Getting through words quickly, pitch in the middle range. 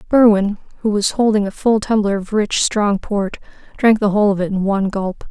No: fast, 215 wpm; high, 205 Hz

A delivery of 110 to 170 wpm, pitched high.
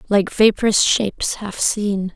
Yes: average, 140 wpm; high, 205 Hz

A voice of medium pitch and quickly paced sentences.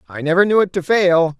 Yes: medium, 175 Hz; fast, 260 wpm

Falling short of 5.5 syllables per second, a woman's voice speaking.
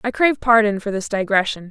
No: 6.2 syllables/s; female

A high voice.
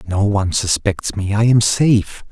No: low, 105 Hz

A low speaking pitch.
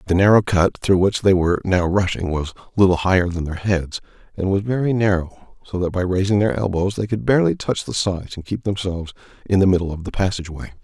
Yes: very low, 95 Hz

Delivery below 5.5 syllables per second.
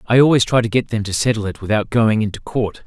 No: 6.2 syllables/s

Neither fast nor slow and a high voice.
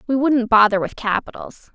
Yes: average, 170 wpm; high, 235 Hz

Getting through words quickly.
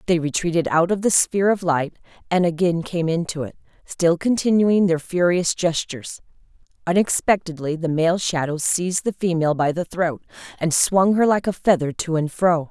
No: average, 175 wpm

